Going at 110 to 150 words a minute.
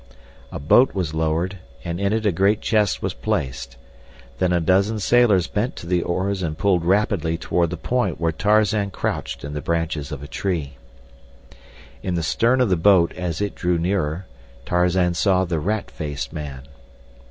No: average, 175 wpm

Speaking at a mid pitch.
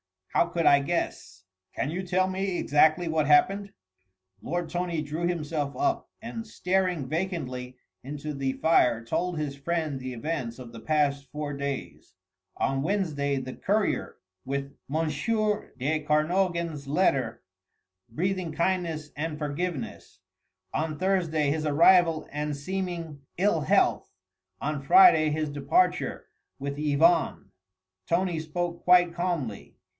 Yes: medium, 155 Hz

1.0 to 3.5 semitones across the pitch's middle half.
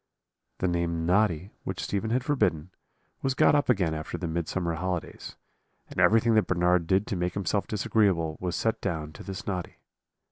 No: average, 4.1 semitones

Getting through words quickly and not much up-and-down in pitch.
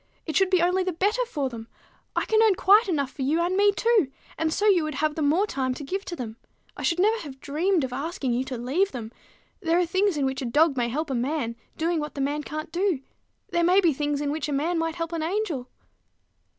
No: fast, 255 wpm; average, 5.1 semitones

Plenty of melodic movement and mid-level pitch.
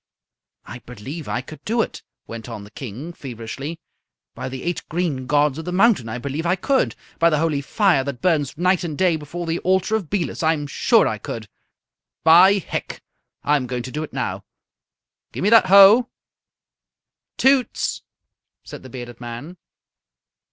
Yes: wide, 5.9 semitones; medium, 155 Hz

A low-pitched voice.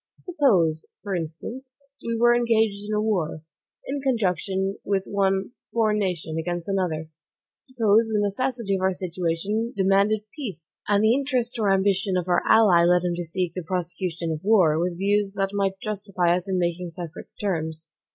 No: high, 195 Hz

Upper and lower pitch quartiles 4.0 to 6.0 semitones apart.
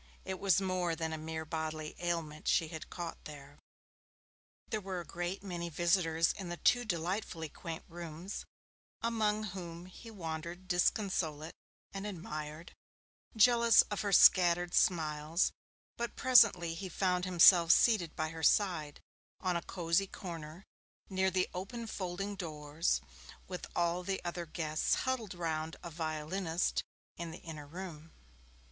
No: average, 2.9 semitones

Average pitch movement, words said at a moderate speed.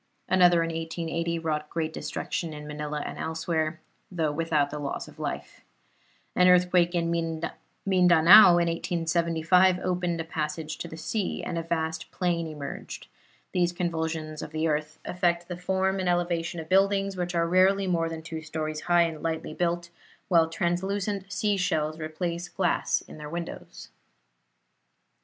No: narrow, 1.9 semitones; average, 150 wpm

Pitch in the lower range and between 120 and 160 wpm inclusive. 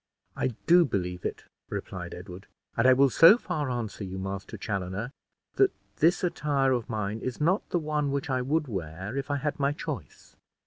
No: low, 130 Hz; average, 185 wpm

